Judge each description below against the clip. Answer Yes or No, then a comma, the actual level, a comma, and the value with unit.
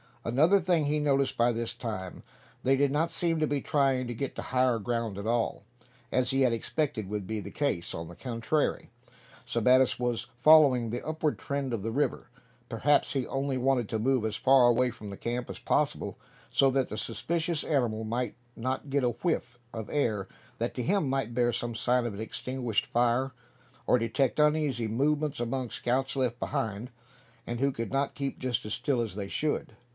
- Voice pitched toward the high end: No, low, 125 Hz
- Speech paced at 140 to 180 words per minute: No, average, 195 wpm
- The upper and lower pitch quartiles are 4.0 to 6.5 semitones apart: No, average, 3.1 semitones